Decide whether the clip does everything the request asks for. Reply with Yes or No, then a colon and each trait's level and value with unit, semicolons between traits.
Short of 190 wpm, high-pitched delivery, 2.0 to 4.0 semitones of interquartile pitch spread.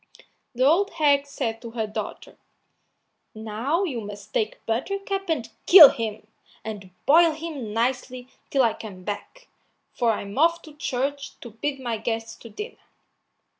No: average, 155 wpm; very high, 250 Hz; wide, 5.4 semitones